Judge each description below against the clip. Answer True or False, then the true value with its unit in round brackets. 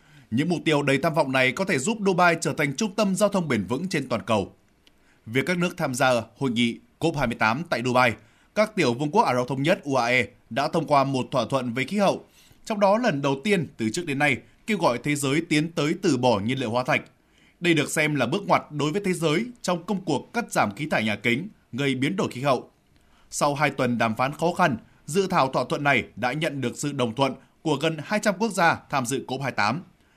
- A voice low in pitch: False (145 Hz)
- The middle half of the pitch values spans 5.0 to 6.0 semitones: True (5.4 semitones)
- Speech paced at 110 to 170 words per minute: False (240 wpm)